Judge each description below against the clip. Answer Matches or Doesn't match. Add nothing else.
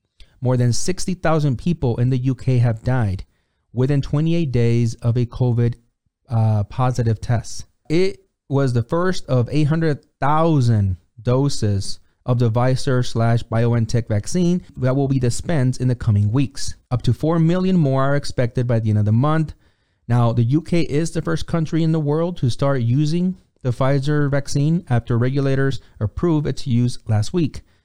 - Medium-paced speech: Matches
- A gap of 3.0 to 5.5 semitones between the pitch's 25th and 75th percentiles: Matches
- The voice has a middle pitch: Doesn't match